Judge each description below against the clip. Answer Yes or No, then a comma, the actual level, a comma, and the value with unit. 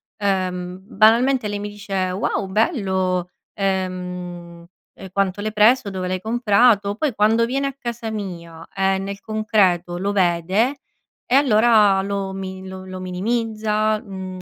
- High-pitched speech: Yes, high, 200 Hz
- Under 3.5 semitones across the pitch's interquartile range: Yes, average, 2.7 semitones